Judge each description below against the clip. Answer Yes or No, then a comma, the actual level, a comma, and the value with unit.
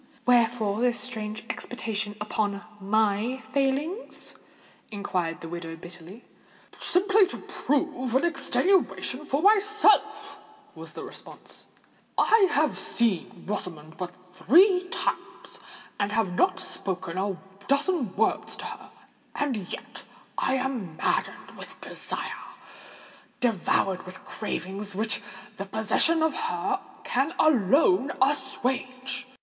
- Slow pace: Yes, slow, 110 wpm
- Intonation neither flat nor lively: No, wide, 7.2 semitones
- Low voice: No, high, 245 Hz